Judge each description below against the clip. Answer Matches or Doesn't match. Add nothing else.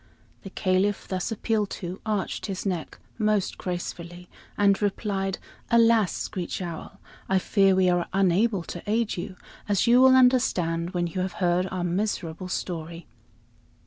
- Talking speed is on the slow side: Doesn't match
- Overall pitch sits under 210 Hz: Matches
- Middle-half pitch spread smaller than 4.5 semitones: Matches